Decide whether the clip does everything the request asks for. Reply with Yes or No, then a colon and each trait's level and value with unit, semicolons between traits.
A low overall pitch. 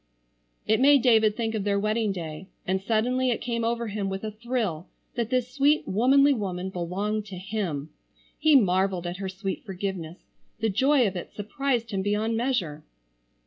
No: high, 215 Hz